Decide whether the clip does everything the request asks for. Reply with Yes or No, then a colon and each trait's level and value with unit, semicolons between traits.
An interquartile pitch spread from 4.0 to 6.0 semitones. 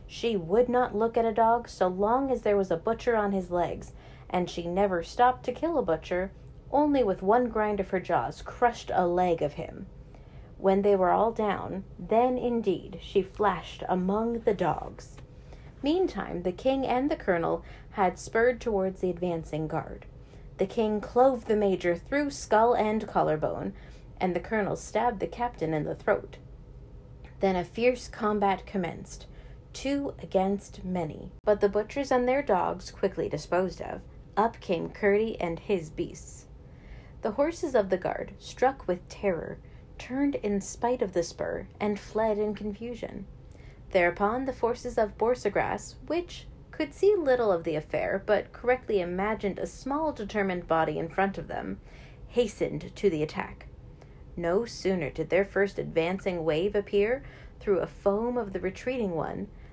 Yes: average, 5.1 semitones